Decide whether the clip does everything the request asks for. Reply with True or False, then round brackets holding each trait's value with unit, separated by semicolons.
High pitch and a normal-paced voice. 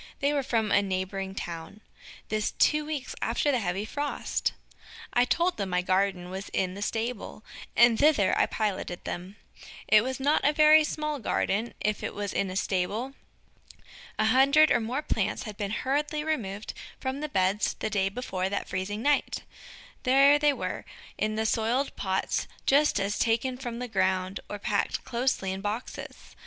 True (220 Hz; 170 wpm)